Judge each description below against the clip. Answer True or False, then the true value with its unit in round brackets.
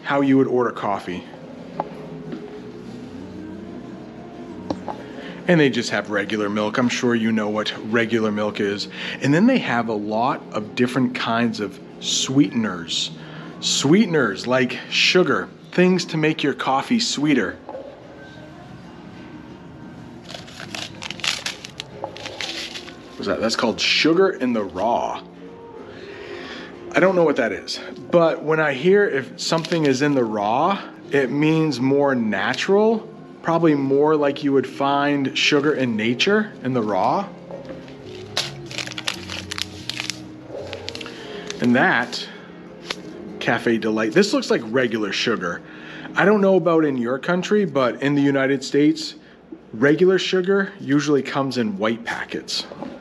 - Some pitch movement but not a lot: False (6.5 semitones)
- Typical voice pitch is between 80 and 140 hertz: True (135 Hz)